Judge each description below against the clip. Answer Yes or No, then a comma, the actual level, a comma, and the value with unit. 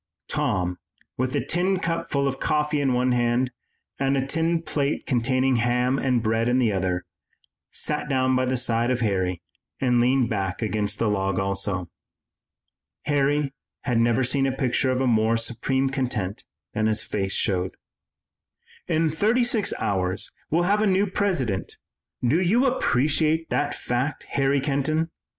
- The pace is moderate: Yes, average, 155 wpm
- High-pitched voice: No, low, 130 Hz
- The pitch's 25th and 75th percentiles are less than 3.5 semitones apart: No, average, 4.6 semitones